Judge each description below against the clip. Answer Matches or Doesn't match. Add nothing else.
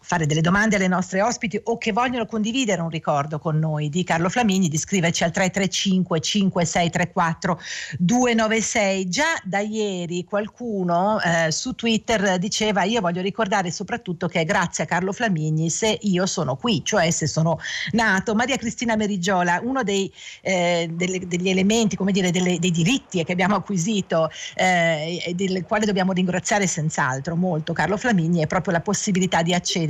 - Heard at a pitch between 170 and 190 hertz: Matches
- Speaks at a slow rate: Doesn't match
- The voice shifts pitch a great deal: Doesn't match